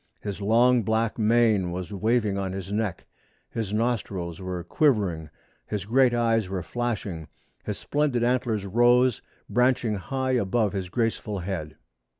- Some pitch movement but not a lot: Yes, average, 4.1 semitones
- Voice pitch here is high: No, low, 110 Hz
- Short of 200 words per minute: Yes, average, 140 wpm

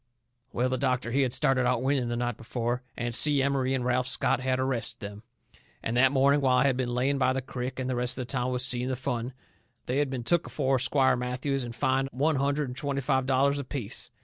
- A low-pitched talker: Yes, low, 130 Hz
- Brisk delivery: Yes, fast, 240 wpm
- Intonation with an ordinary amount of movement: No, narrow, 1.6 semitones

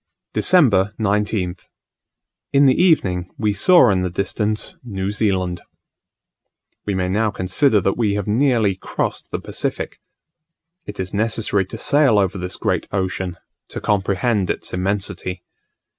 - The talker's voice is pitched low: Yes, low, 100 Hz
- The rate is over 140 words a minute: No, slow, 135 wpm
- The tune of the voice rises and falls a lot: No, average, 3.1 semitones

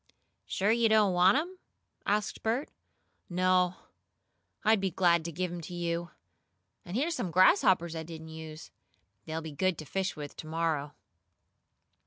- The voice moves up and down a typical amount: Yes, average, 3.3 semitones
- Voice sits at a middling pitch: Yes, medium, 175 Hz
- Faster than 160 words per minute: No, average, 155 wpm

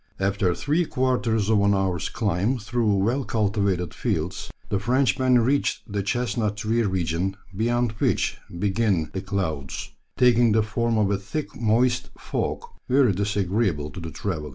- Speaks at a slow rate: No, average, 150 wpm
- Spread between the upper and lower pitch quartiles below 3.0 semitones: No, average, 3.8 semitones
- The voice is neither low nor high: No, low, 105 Hz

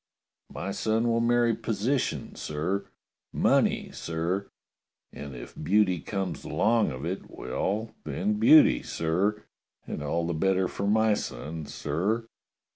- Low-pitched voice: Yes, low, 100 Hz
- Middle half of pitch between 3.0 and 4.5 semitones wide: No, average, 5.3 semitones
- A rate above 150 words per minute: No, slow, 135 wpm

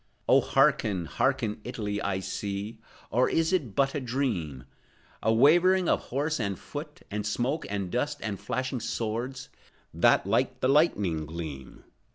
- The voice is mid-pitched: No, low, 115 Hz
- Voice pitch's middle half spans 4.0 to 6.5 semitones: Yes, average, 5.3 semitones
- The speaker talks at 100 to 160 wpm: Yes, average, 150 wpm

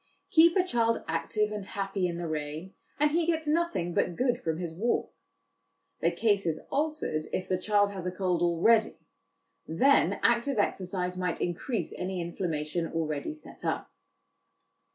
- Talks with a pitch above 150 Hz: Yes, high, 190 Hz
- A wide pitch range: Yes, wide, 5.9 semitones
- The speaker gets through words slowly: No, average, 155 wpm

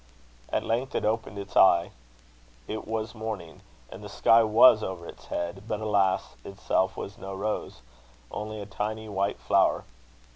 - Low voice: Yes, low, 105 Hz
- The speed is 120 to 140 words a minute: No, average, 155 wpm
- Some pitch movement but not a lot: No, narrow, 2.2 semitones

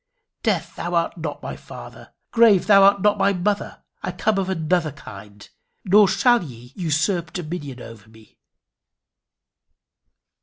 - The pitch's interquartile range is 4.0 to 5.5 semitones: Yes, average, 5.2 semitones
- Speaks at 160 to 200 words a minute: No, average, 140 wpm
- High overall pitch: No, medium, 175 Hz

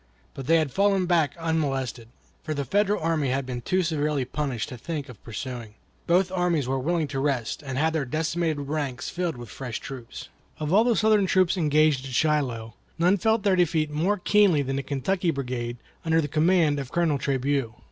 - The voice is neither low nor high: Yes, medium, 150 Hz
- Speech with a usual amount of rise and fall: Yes, average, 4.5 semitones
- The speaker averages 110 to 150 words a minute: No, average, 195 wpm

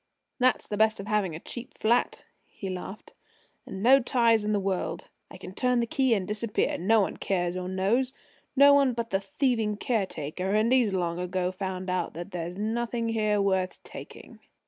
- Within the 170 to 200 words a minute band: Yes, average, 190 wpm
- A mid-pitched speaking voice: No, high, 210 Hz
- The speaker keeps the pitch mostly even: No, average, 3.8 semitones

